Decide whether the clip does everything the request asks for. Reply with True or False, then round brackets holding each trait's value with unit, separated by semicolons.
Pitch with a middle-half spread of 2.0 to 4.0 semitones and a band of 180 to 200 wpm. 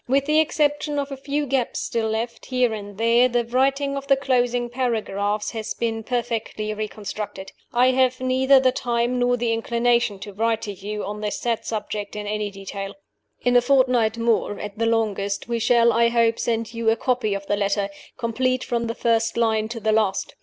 True (2.8 semitones; 195 wpm)